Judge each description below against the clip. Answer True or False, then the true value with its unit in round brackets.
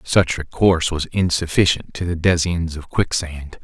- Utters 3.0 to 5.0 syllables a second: True (4.9 syllables/s)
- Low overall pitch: True (85 Hz)